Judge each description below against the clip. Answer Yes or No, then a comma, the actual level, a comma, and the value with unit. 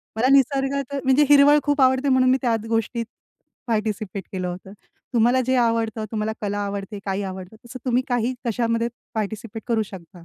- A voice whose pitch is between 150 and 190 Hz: No, high, 230 Hz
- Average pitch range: Yes, average, 3.7 semitones